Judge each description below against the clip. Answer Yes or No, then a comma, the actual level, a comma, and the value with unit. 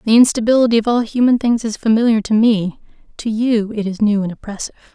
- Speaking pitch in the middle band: No, high, 220 Hz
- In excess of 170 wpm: Yes, fast, 205 wpm